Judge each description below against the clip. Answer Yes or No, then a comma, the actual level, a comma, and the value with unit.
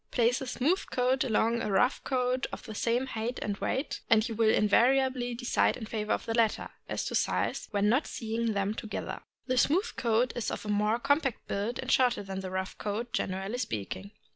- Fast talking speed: Yes, fast, 210 wpm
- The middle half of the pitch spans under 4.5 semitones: Yes, average, 3.1 semitones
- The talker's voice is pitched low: No, high, 230 Hz